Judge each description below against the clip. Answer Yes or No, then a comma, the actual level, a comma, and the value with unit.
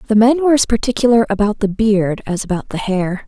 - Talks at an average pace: No, fast, 220 wpm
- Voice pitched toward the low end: No, high, 215 Hz